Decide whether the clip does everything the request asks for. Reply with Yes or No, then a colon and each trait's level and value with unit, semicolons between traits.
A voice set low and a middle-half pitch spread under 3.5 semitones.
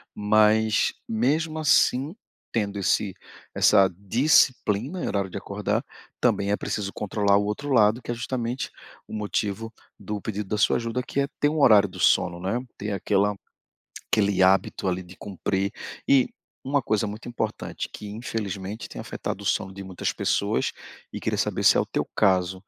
Yes: low, 105 Hz; average, 3.1 semitones